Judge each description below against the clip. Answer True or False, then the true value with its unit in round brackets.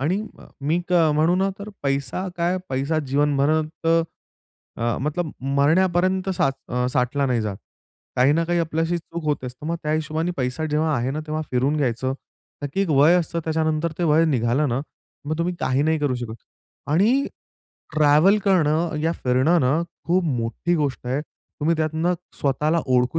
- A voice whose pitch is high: False (155 Hz)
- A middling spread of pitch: True (3.4 semitones)